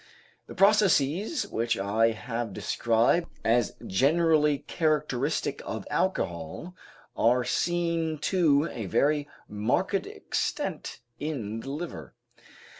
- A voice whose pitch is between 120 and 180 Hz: Yes, medium, 140 Hz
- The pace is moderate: No, slow, 100 wpm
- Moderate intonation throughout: No, wide, 6.3 semitones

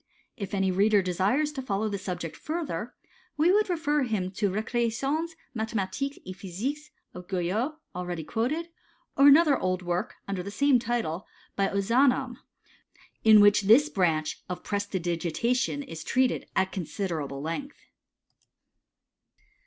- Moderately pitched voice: No, high, 210 Hz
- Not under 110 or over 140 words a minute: Yes, slow, 135 wpm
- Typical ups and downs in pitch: No, wide, 6.7 semitones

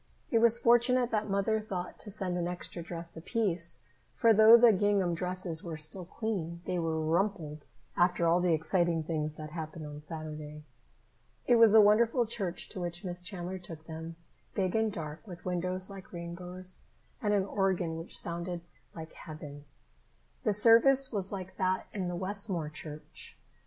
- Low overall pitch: No, medium, 180 Hz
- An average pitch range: Yes, average, 3.7 semitones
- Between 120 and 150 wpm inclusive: No, average, 165 wpm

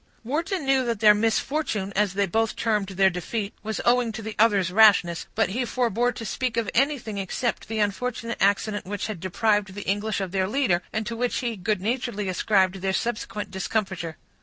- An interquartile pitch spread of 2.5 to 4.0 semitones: Yes, average, 3.2 semitones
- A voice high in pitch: Yes, high, 215 Hz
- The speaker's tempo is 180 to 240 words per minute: Yes, average, 190 wpm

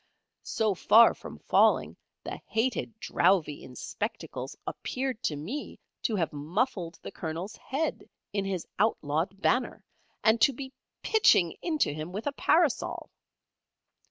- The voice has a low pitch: No, high, 210 Hz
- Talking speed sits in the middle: No, slow, 130 wpm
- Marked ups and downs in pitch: Yes, wide, 7.4 semitones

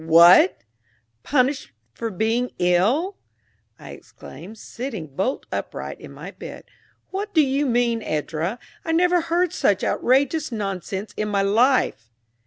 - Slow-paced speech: Yes, slow, 130 wpm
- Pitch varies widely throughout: Yes, wide, 7.1 semitones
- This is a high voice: Yes, high, 230 Hz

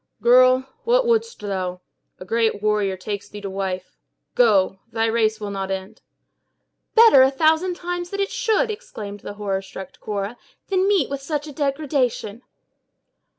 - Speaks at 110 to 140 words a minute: No, average, 150 wpm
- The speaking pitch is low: No, high, 230 Hz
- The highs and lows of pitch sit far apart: Yes, wide, 7.9 semitones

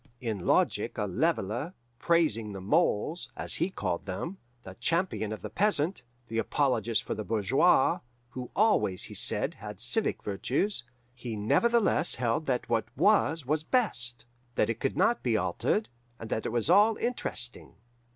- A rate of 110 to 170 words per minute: Yes, average, 160 wpm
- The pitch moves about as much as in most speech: No, wide, 8.0 semitones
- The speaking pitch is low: Yes, low, 125 Hz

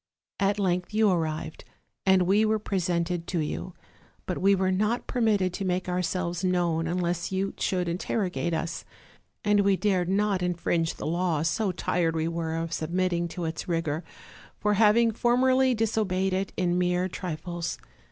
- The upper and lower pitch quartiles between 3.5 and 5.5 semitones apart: No, narrow, 2.6 semitones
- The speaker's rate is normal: Yes, average, 160 wpm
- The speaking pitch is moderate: Yes, medium, 180 Hz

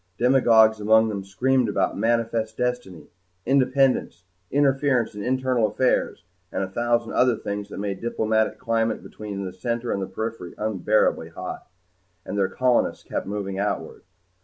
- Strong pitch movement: No, average, 3.4 semitones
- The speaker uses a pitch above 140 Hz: No, low, 110 Hz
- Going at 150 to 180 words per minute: No, average, 140 wpm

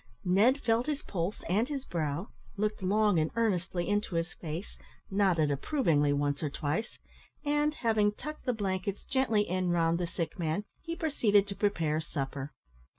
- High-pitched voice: Yes, high, 195 Hz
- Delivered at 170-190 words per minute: No, average, 160 wpm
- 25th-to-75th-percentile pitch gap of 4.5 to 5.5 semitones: Yes, average, 5.2 semitones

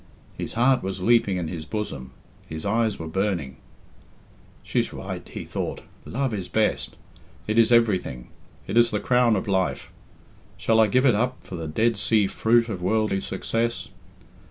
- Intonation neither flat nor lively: Yes, average, 3.8 semitones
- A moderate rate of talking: Yes, average, 165 wpm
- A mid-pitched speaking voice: No, low, 110 Hz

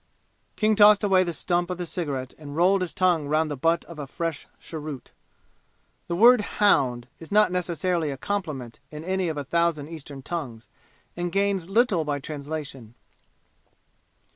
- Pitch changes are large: No, average, 4.2 semitones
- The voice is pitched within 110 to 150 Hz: No, medium, 165 Hz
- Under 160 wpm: No, average, 165 wpm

